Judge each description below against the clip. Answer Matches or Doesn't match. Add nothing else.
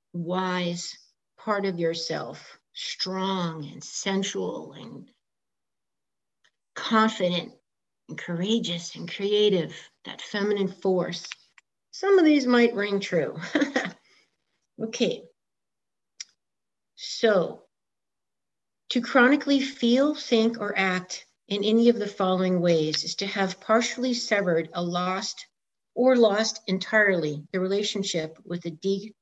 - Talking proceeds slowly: Matches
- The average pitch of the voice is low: Doesn't match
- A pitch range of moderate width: Matches